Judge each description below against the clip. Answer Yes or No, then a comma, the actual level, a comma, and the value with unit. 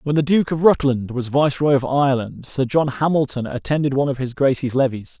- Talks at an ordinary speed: No, fast, 210 wpm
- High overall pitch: No, low, 135 Hz